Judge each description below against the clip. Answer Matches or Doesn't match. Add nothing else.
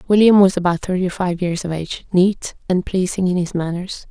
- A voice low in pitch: Doesn't match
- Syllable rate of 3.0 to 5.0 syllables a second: Doesn't match